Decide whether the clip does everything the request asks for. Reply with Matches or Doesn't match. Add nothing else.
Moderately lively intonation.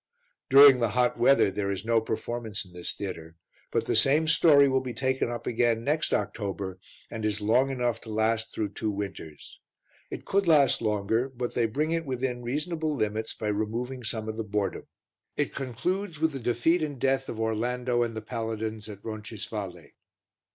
Matches